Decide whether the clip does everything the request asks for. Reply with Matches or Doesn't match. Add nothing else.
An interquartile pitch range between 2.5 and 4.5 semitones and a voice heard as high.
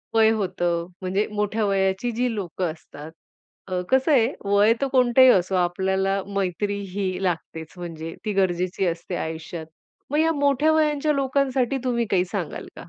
Doesn't match